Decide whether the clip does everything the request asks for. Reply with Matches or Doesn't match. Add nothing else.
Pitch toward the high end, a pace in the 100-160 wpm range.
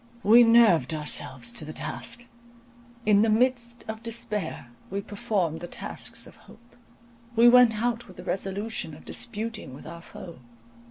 Matches